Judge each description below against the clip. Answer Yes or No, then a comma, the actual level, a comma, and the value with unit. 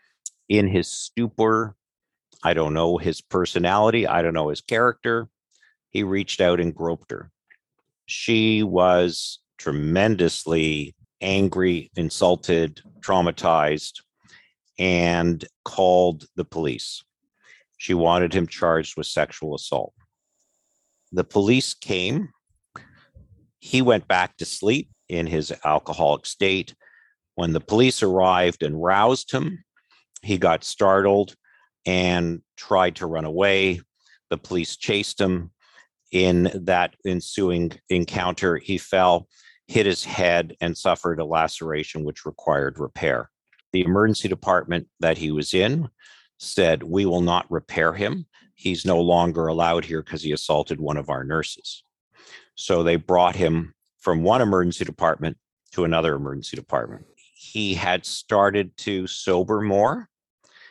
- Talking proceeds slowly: Yes, slow, 125 wpm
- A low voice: Yes, very low, 90 Hz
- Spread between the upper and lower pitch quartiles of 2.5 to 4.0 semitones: Yes, average, 3.0 semitones